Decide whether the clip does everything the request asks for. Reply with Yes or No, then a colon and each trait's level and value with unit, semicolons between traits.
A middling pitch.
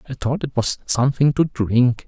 No: low, 130 Hz